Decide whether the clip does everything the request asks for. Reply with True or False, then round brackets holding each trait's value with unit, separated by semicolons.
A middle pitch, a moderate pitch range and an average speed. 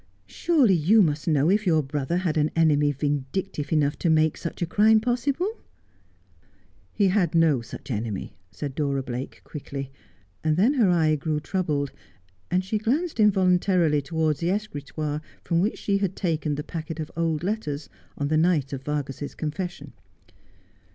True (160 Hz; 4.4 semitones; 170 wpm)